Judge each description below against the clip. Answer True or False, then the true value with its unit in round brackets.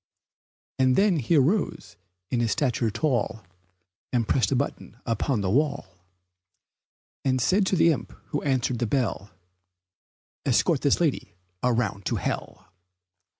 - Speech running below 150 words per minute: True (135 wpm)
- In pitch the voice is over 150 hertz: False (125 Hz)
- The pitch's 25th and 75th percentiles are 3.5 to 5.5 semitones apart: True (4.2 semitones)